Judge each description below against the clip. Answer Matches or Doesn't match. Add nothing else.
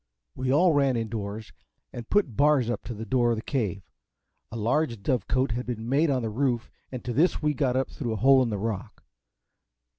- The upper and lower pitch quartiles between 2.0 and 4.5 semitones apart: Matches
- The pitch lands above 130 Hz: Doesn't match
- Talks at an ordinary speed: Doesn't match